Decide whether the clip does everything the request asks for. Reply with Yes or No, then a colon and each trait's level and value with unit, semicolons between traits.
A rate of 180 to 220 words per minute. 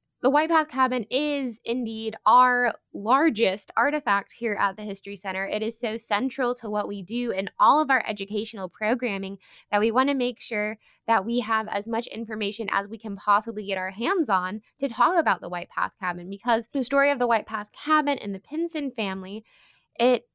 Yes: average, 200 wpm